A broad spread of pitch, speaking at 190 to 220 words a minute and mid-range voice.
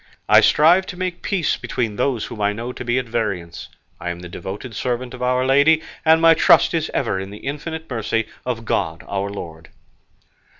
No: wide, 6.6 semitones; average, 200 wpm; low, 120 Hz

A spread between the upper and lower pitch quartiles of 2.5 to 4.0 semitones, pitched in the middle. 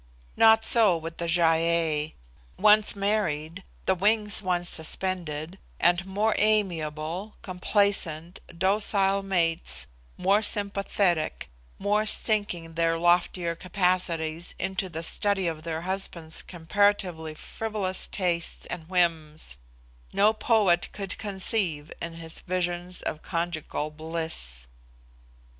Yes: average, 3.4 semitones; medium, 175 Hz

